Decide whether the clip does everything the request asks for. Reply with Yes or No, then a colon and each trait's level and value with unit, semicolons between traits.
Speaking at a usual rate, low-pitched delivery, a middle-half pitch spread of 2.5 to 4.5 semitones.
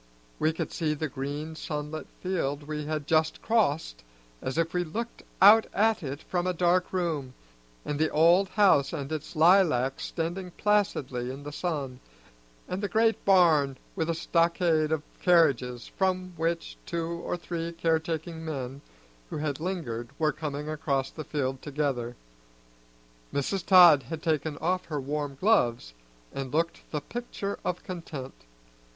No: average, 155 wpm; medium, 160 Hz; average, 3.6 semitones